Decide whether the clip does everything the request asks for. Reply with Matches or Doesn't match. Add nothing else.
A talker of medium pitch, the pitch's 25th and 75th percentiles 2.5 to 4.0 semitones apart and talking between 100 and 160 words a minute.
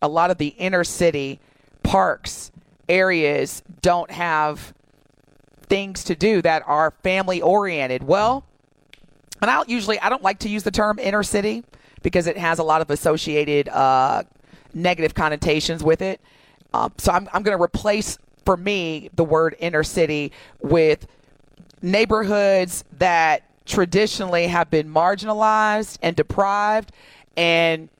Doesn't match